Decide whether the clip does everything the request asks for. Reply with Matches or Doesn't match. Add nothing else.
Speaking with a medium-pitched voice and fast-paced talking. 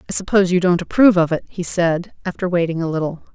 Matches